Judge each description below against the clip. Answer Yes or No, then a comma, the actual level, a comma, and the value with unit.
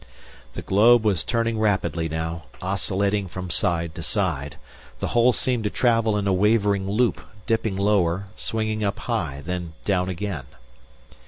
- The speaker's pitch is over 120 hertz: No, low, 100 Hz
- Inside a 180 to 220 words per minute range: No, average, 150 wpm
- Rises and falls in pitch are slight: No, average, 3.8 semitones